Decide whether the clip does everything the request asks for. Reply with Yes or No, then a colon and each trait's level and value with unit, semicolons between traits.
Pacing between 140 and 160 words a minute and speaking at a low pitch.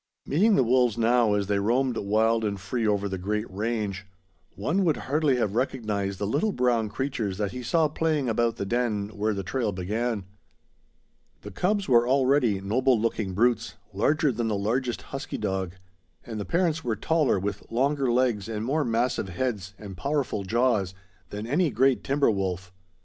No: average, 175 wpm; low, 115 Hz